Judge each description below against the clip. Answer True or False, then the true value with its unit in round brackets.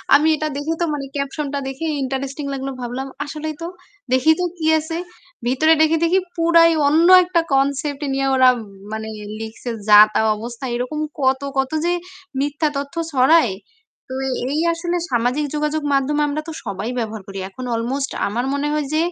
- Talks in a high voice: True (280 Hz)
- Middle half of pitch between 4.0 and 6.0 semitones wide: False (3.3 semitones)